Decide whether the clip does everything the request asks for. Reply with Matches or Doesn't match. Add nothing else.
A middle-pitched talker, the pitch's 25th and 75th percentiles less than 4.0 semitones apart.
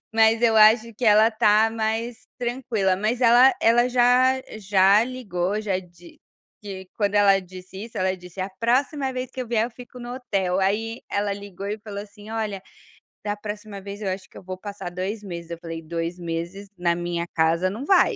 Doesn't match